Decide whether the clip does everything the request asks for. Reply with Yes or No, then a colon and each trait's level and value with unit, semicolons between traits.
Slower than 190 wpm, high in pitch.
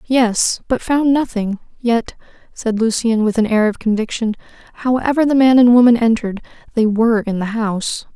Yes: average, 170 wpm; high, 230 Hz